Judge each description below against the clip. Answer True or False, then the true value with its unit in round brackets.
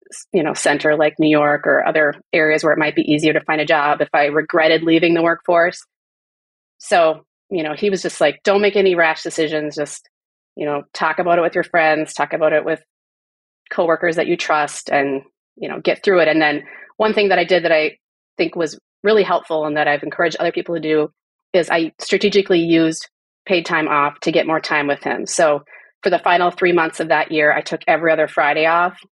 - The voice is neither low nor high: True (160 Hz)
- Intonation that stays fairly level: True (2.2 semitones)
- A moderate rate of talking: False (220 wpm)